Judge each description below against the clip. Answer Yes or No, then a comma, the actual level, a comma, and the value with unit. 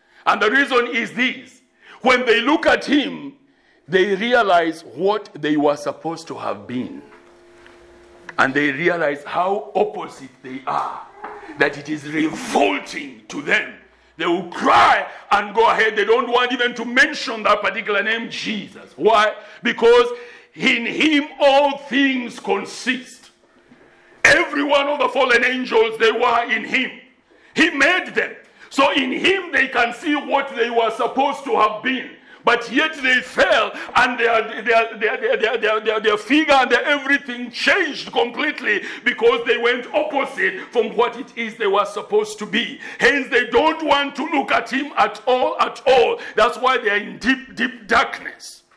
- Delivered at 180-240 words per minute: No, average, 165 wpm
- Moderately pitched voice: No, very high, 250 Hz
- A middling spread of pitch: Yes, average, 4.1 semitones